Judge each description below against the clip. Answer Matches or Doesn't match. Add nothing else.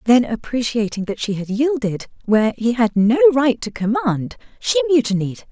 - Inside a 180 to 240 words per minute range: Doesn't match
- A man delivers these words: Doesn't match